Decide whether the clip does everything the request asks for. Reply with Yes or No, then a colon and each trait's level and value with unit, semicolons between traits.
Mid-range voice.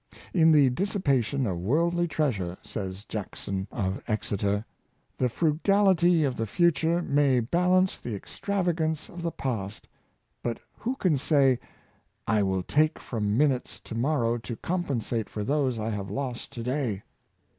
No: low, 130 Hz